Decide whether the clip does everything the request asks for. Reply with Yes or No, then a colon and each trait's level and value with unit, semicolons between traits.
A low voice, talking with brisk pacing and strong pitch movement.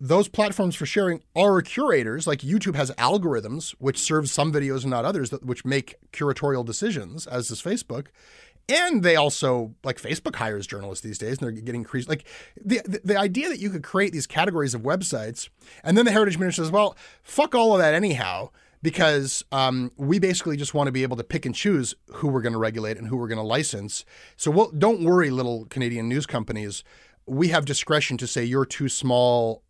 No: medium, 145 Hz; fast, 210 wpm; wide, 7.0 semitones